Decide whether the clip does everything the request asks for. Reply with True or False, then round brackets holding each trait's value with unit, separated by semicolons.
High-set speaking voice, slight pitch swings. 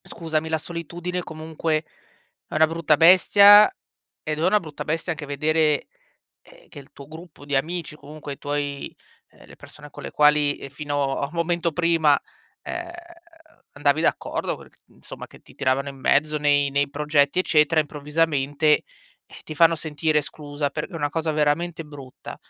False (155 Hz; 2.3 semitones)